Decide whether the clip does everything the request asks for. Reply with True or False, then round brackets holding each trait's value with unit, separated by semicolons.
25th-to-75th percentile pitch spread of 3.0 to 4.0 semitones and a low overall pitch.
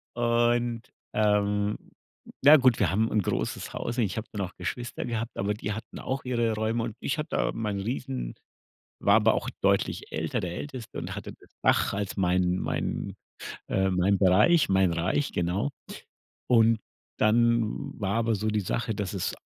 True (3.3 semitones; 110 Hz)